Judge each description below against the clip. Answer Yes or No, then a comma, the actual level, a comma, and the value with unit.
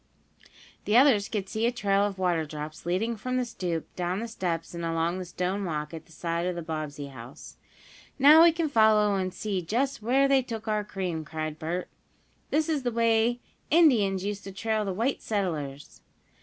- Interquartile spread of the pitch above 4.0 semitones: Yes, wide, 5.4 semitones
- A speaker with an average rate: Yes, average, 195 wpm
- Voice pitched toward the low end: No, high, 195 Hz